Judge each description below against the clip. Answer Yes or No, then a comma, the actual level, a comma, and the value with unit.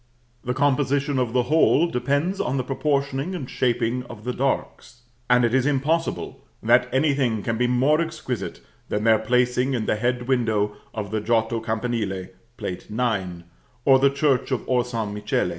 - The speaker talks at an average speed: Yes, average, 170 wpm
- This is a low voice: Yes, low, 125 Hz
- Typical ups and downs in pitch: Yes, average, 3.3 semitones